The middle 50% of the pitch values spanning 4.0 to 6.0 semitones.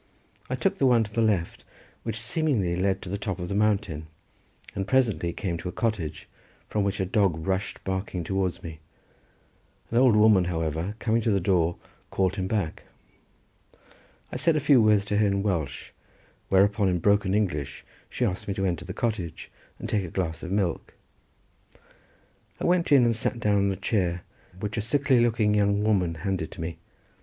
No: average, 3.4 semitones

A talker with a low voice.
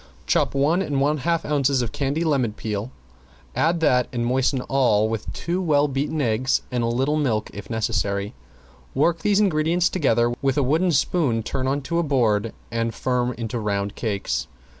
Yes: low, 130 Hz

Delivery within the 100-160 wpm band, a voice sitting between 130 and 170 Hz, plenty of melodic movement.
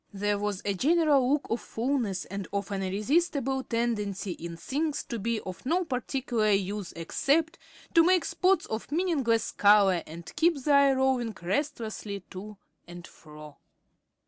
No: average, 150 wpm; high, 230 Hz; wide, 6.2 semitones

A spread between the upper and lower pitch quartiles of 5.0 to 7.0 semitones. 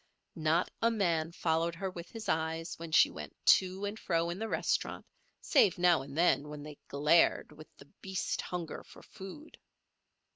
No: average, 2.9 semitones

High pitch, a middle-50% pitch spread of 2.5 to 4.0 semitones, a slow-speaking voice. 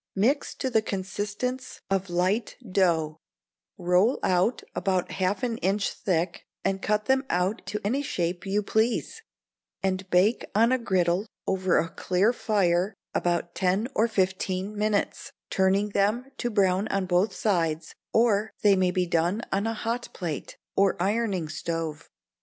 No: high, 195 Hz; average, 3.2 semitones; average, 150 wpm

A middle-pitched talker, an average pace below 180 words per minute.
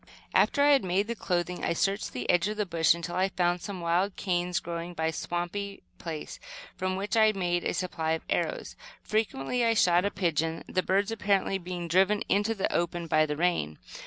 No: medium, 180 Hz; fast, 205 wpm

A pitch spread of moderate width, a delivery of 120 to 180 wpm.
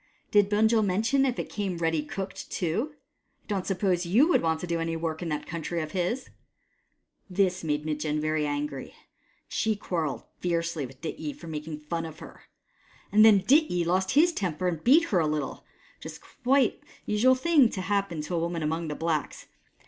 No: average, 4.7 semitones; average, 200 wpm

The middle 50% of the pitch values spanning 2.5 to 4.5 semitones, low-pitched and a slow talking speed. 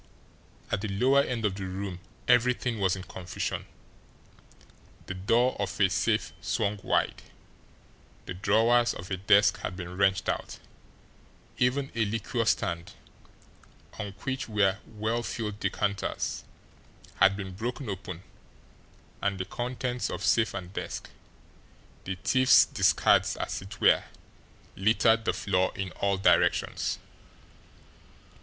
Yes: average, 3.5 semitones; low, 100 Hz; slow, 125 wpm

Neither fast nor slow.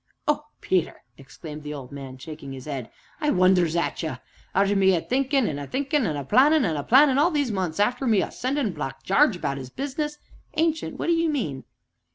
No: fast, 215 wpm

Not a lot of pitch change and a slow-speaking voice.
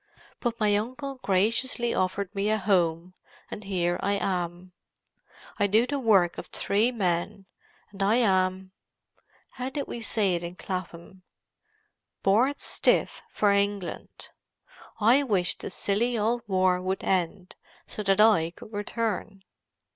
No: average, 3.4 semitones; slow, 130 wpm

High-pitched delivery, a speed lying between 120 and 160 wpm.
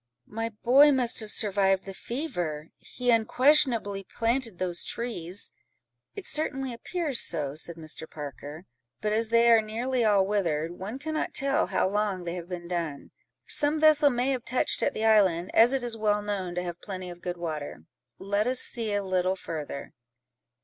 No: high, 210 Hz; average, 175 wpm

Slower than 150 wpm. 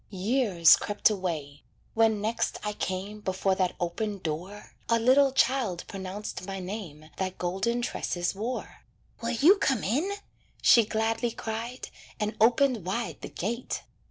Yes: average, 140 wpm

